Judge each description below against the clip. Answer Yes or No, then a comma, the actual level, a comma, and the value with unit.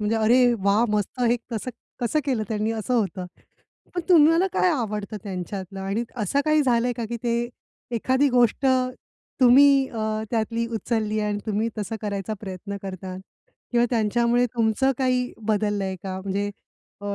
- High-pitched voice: Yes, high, 225 Hz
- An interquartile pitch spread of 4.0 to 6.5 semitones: No, average, 3.2 semitones